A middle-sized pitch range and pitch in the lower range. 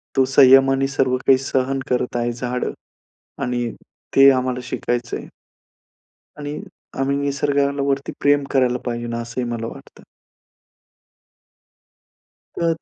No: narrow, 2.0 semitones; low, 130 Hz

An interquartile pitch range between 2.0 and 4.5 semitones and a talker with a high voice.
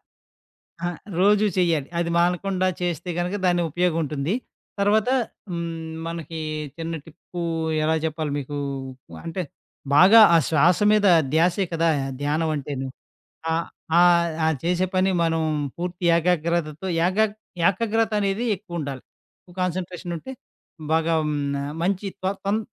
No: narrow, 2.6 semitones; medium, 170 Hz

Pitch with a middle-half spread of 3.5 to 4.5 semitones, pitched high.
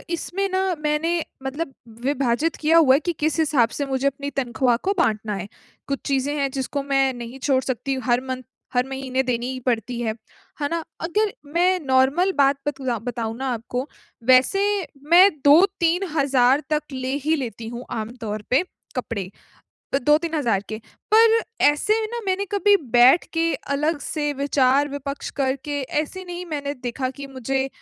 Yes: average, 4.1 semitones; very high, 275 Hz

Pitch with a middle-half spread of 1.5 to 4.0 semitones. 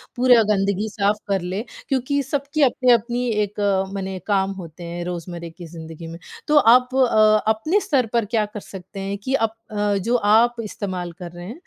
No: average, 4.6 semitones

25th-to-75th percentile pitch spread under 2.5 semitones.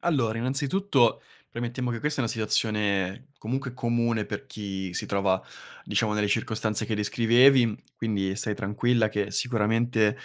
No: average, 2.8 semitones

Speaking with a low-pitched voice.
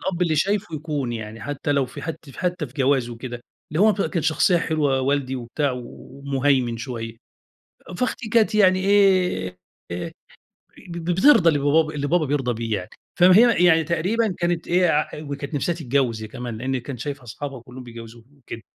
No: medium, 145 Hz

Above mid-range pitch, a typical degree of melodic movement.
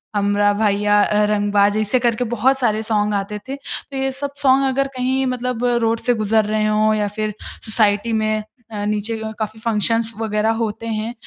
No: high, 215 Hz; narrow, 2.1 semitones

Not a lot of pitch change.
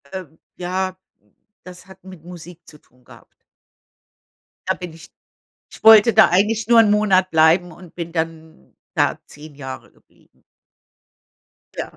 No: average, 3.0 semitones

